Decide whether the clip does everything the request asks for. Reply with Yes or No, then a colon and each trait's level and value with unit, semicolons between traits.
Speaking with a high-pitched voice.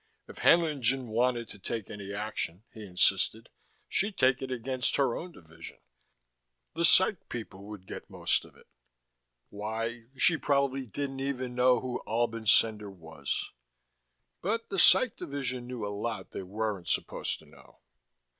No: low, 120 Hz